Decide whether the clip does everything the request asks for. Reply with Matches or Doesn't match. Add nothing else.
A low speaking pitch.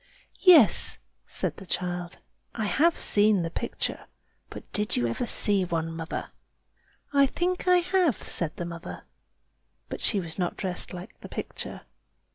Doesn't match